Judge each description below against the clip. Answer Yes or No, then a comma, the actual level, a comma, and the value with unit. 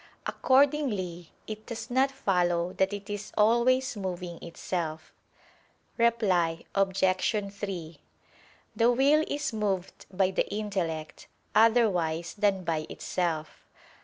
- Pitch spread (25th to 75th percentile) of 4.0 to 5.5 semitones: Yes, average, 4.6 semitones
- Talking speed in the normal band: No, slow, 105 wpm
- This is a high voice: Yes, high, 195 Hz